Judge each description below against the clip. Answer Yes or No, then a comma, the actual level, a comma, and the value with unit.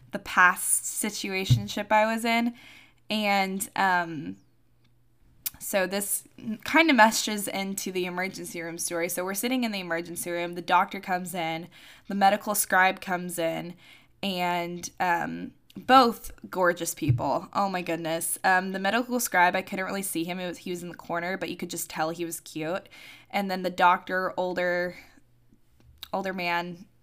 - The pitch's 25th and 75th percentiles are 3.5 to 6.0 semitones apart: No, narrow, 2.6 semitones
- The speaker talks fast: No, average, 160 wpm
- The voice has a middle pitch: Yes, medium, 180 Hz